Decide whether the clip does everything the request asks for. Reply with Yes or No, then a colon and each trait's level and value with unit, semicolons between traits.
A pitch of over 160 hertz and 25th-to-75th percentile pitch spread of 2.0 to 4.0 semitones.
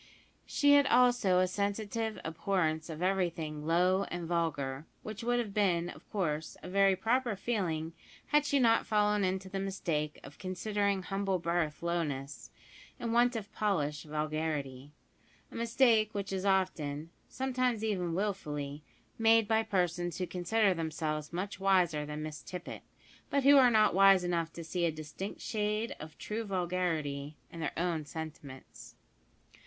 No: medium, 185 Hz; average, 4.8 semitones